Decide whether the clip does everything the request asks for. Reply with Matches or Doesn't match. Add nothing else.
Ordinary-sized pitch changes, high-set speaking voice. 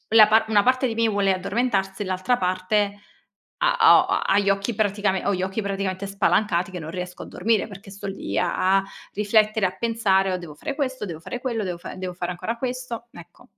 Matches